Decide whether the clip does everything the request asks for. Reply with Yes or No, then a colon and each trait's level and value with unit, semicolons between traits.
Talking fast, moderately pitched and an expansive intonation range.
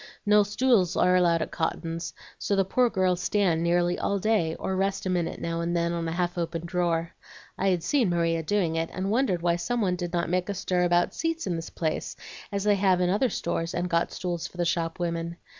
No: fast, 225 wpm; medium, 175 Hz; narrow, 2.4 semitones